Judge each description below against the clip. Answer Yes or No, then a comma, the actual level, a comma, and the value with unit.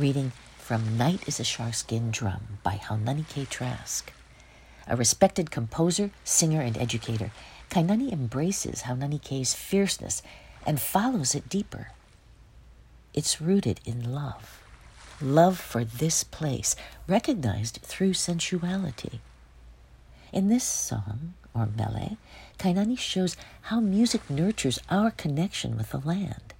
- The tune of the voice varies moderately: No, wide, 8.1 semitones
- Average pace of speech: No, slow, 115 wpm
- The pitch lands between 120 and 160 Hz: Yes, medium, 140 Hz